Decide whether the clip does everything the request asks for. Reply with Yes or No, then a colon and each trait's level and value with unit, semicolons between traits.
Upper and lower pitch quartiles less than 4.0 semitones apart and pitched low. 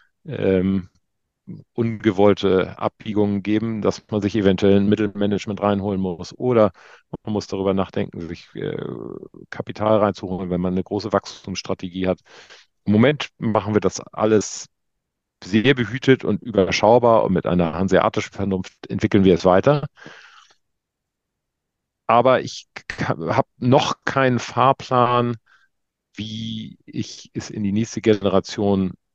Yes: average, 2.7 semitones; low, 100 Hz